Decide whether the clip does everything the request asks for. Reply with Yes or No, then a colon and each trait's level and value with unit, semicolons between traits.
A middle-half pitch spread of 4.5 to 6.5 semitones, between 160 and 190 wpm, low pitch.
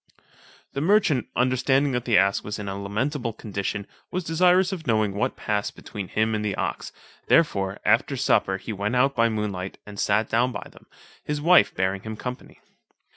Yes: average, 5.2 semitones; average, 180 wpm; low, 110 Hz